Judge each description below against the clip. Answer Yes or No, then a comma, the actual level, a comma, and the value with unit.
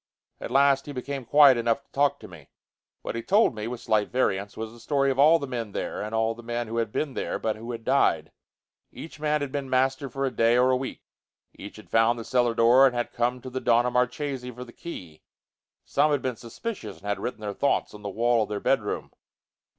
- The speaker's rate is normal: No, fast, 240 wpm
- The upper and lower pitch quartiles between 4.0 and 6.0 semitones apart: No, average, 3.1 semitones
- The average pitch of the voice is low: Yes, low, 125 Hz